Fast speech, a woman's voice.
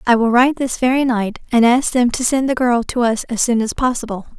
Yes: fast, 260 wpm; female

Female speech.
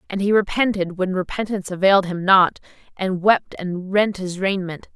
Yes: female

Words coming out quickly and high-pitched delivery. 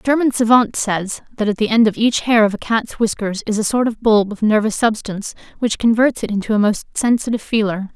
Yes: fast, 235 wpm; high, 220 Hz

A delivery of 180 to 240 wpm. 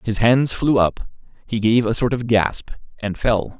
Yes: average, 200 wpm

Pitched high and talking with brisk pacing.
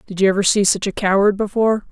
Yes: high, 200 Hz; fast, 250 wpm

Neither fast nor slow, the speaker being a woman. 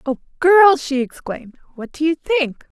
Yes: average, 170 wpm; female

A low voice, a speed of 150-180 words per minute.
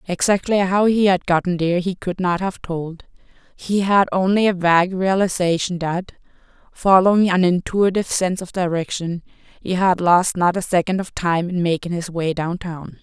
No: medium, 180 Hz; average, 170 wpm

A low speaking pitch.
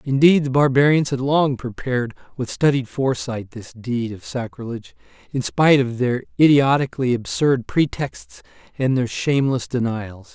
Yes: low, 130 Hz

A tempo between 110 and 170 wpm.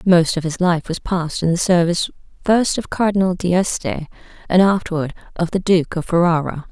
No: average, 180 wpm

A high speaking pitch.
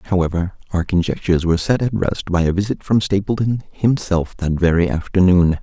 No: very low, 95 Hz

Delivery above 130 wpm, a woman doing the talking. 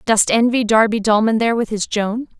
Yes: average, 200 wpm; female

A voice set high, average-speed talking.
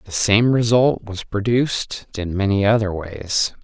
No: low, 105 Hz; average, 150 wpm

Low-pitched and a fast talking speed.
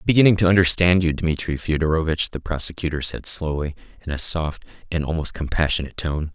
No: very low, 80 Hz; average, 180 wpm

